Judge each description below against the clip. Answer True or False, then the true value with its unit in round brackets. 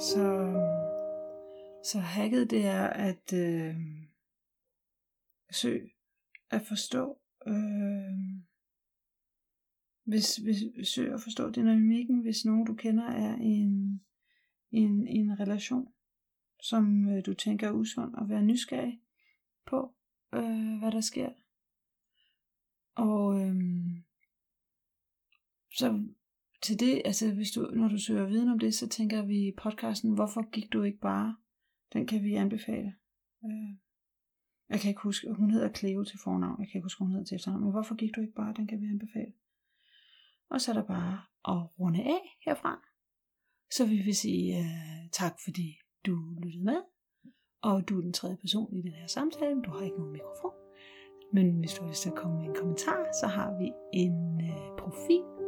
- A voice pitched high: True (210 Hz)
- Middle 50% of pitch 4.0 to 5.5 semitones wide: False (2.9 semitones)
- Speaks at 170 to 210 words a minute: False (155 wpm)